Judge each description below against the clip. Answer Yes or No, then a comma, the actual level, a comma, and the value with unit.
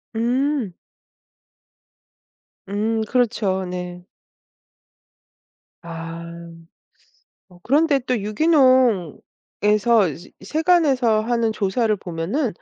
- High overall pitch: Yes, high, 220 Hz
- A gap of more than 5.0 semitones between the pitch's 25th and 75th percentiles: Yes, wide, 5.4 semitones